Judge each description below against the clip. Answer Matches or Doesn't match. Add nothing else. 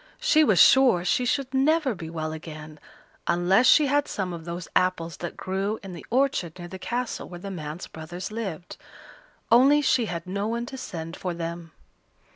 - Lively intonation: Matches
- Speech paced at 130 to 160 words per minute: Doesn't match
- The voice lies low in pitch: Doesn't match